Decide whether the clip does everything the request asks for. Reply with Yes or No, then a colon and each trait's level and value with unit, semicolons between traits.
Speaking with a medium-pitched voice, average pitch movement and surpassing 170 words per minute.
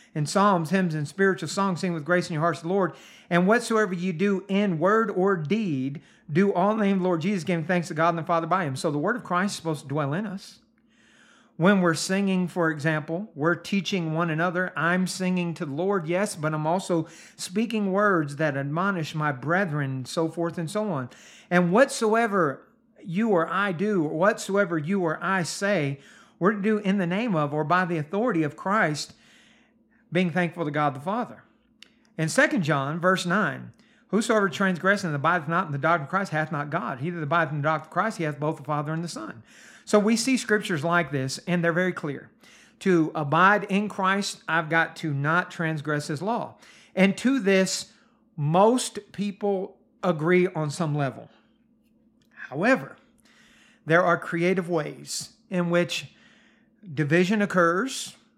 Yes: medium, 180 Hz; average, 4.0 semitones; average, 190 wpm